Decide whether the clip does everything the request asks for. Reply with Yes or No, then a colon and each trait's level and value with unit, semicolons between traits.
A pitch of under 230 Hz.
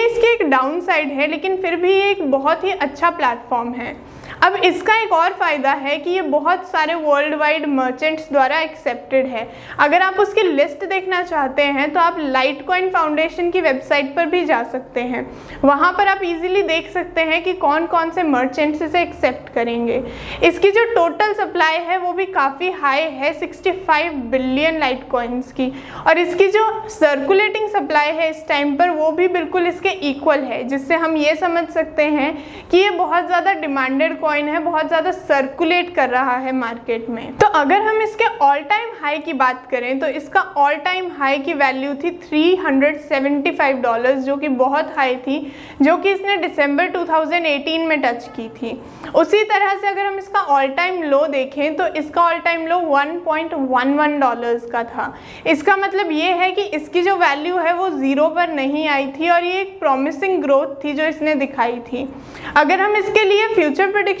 No: very high, 315 Hz